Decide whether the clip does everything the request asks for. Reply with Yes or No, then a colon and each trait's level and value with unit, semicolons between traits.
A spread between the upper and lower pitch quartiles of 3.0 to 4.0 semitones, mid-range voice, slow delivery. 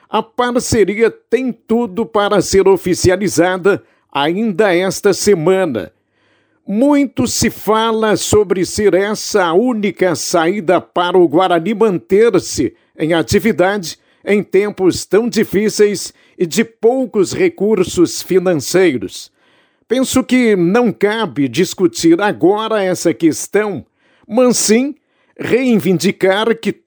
No: average, 3.7 semitones; high, 205 Hz; slow, 105 wpm